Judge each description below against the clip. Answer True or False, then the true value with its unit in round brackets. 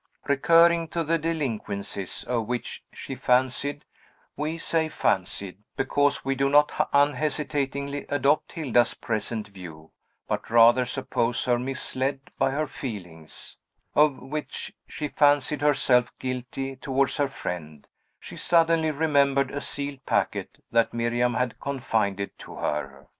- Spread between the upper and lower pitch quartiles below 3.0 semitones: False (3.7 semitones)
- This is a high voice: False (135 Hz)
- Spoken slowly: True (125 wpm)